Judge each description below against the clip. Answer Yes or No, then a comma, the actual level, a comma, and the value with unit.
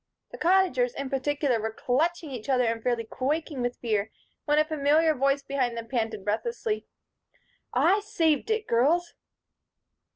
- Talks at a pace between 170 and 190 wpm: No, average, 150 wpm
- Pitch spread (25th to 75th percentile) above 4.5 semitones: Yes, average, 5.1 semitones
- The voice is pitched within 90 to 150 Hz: No, very high, 275 Hz